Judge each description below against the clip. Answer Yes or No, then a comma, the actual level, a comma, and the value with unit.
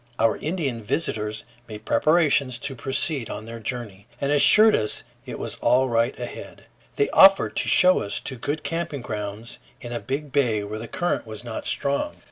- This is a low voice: Yes, low, 125 Hz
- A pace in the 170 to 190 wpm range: Yes, average, 180 wpm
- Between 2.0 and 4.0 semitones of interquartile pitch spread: No, average, 4.6 semitones